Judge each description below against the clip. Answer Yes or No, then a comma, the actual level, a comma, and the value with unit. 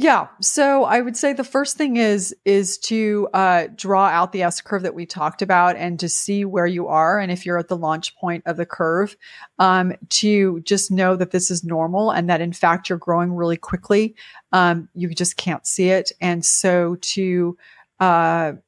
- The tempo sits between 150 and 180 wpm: No, average, 200 wpm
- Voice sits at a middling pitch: Yes, medium, 180 Hz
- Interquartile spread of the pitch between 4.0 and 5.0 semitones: No, narrow, 2.5 semitones